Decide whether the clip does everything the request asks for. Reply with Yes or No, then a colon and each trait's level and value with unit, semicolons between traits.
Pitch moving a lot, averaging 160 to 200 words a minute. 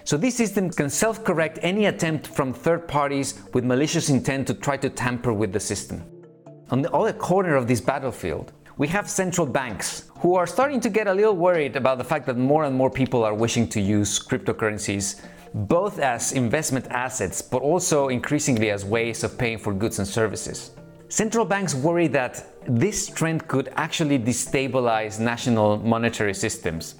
Yes: wide, 6.1 semitones; average, 180 wpm